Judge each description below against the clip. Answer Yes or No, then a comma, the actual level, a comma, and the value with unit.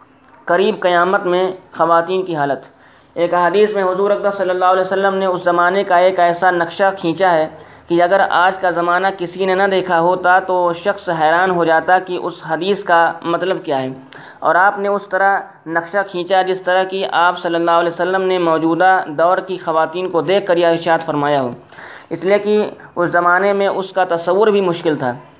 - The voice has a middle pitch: Yes, medium, 180 Hz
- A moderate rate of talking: No, fast, 200 wpm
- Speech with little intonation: Yes, narrow, 2.1 semitones